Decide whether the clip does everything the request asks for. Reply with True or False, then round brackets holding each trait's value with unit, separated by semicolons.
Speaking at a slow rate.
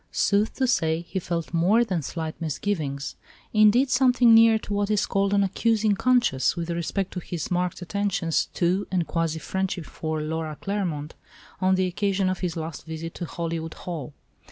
False (175 wpm)